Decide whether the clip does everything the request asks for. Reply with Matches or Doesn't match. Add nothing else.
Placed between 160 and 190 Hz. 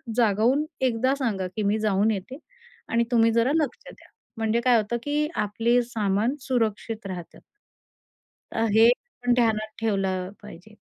Doesn't match